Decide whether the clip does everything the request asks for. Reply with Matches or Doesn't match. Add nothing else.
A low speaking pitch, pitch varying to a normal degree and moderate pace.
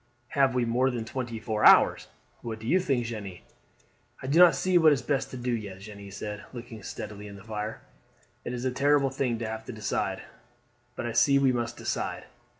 Doesn't match